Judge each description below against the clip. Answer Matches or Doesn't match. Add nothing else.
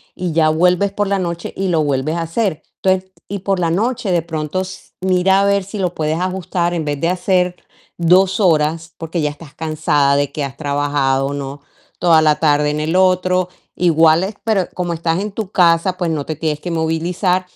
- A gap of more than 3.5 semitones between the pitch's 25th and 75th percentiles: Doesn't match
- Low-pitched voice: Doesn't match